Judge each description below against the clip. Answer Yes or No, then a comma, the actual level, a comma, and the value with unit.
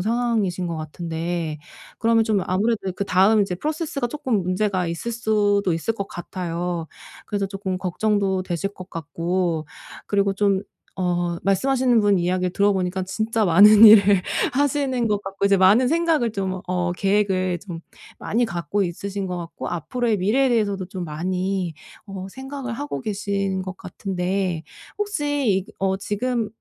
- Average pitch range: Yes, average, 3.4 semitones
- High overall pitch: Yes, high, 195 Hz